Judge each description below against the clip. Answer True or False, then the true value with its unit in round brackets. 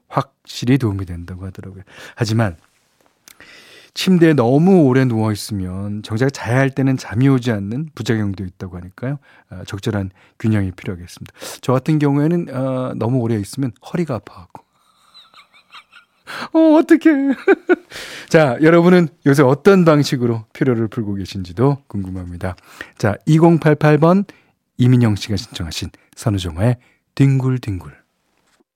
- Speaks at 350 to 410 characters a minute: False (290 characters per minute)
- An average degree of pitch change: False (7.0 semitones)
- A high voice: False (125 Hz)